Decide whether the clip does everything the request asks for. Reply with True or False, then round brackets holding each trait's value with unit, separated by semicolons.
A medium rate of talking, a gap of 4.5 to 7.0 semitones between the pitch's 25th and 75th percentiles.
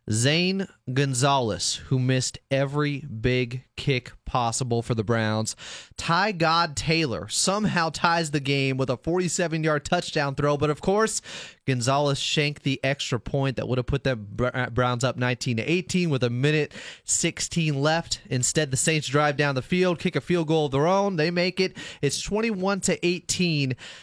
True (165 wpm; 4.8 semitones)